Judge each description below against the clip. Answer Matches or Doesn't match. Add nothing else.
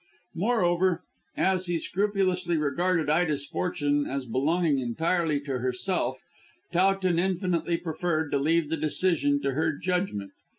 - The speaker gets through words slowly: Matches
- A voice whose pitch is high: Doesn't match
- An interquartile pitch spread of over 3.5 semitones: Matches